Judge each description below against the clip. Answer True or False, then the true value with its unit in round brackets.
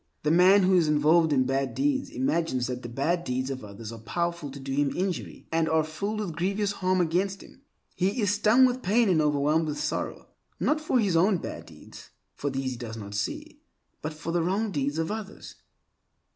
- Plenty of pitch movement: True (5.9 semitones)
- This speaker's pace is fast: True (210 wpm)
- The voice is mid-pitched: True (165 Hz)